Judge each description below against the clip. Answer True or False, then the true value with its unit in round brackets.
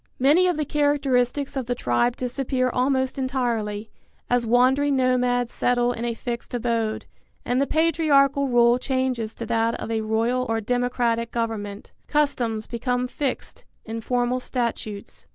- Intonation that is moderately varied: False (2.3 semitones)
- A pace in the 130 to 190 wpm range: True (145 wpm)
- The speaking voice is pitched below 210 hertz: False (245 Hz)